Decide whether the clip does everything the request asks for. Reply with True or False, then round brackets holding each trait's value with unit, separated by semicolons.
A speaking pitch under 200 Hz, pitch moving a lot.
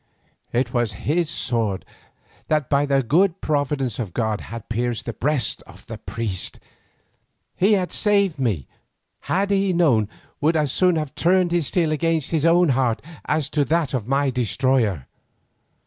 True (140 Hz; 5.7 semitones)